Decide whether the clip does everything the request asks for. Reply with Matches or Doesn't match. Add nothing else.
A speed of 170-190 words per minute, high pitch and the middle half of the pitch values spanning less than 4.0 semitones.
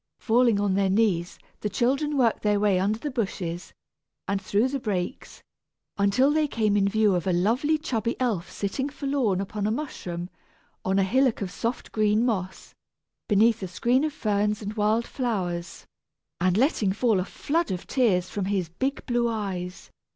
Doesn't match